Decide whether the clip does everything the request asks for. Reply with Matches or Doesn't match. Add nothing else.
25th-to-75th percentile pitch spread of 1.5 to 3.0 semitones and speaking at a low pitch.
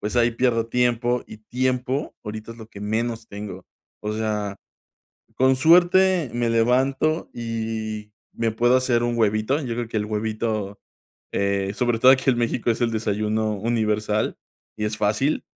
Matches